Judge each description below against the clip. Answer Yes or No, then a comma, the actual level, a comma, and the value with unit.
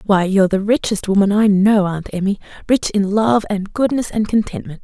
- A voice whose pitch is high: Yes, high, 200 Hz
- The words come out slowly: No, average, 200 wpm